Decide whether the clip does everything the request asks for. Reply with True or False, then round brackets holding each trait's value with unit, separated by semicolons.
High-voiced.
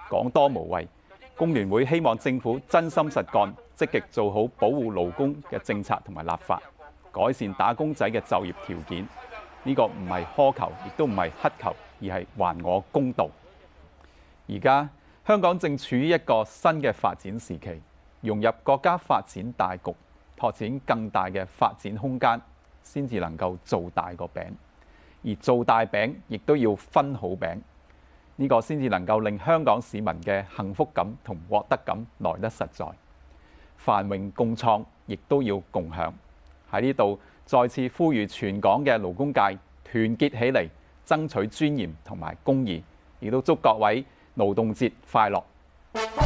False (105 Hz)